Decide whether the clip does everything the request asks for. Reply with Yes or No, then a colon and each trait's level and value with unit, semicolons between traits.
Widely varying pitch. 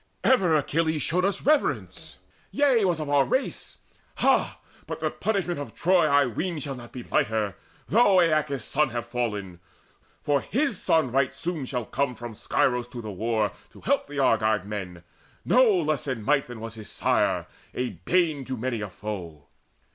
Yes: wide, 6.9 semitones